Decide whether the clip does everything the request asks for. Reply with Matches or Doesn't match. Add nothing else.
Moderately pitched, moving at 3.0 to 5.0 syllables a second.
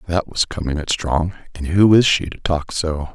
Doesn't match